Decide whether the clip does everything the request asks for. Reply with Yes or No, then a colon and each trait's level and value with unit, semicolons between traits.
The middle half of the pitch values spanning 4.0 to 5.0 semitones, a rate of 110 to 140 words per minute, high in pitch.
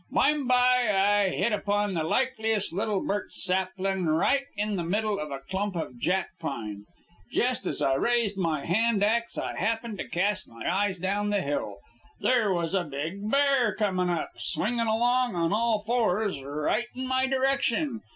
No: average, 4.7 semitones; average, 170 wpm; high, 205 Hz